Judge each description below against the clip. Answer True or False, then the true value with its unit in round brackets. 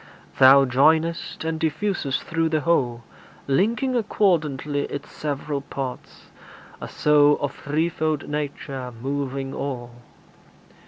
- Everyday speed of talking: False (105 wpm)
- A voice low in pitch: False (145 Hz)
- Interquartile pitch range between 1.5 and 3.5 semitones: True (3.0 semitones)